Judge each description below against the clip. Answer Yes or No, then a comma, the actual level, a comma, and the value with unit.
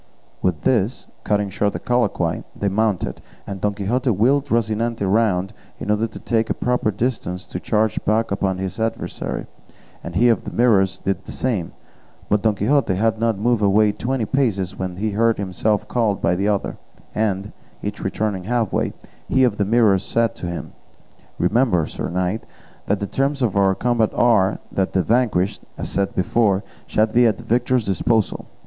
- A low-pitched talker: Yes, low, 105 Hz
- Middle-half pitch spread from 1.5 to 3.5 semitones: Yes, average, 3.1 semitones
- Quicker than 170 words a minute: Yes, average, 180 wpm